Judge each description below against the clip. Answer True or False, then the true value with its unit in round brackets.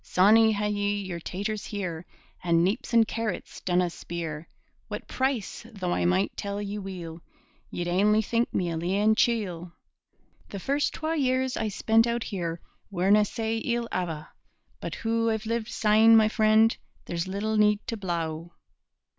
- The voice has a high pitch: True (205 Hz)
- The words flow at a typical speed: True (160 wpm)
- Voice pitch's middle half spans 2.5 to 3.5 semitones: False (4.0 semitones)